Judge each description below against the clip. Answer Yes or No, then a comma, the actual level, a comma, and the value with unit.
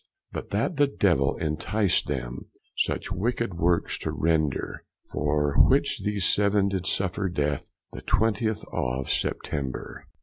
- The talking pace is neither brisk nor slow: No, slow, 130 wpm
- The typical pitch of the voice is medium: No, very low, 90 Hz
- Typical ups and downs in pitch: No, wide, 5.8 semitones